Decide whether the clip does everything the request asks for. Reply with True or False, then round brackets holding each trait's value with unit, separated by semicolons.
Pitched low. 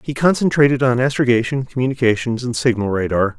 True (125 Hz)